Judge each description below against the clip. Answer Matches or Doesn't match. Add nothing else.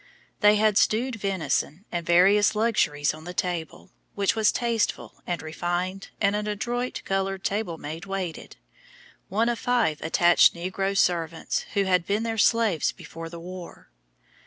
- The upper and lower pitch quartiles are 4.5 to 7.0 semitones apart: Doesn't match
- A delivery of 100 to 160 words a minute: Matches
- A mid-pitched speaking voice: Doesn't match